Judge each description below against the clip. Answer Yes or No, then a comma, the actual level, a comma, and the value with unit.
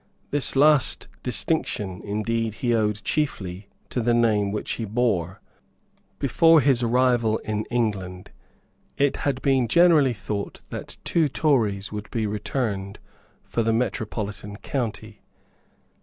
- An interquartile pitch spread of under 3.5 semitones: No, average, 3.8 semitones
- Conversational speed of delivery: No, slow, 125 wpm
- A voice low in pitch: Yes, low, 115 Hz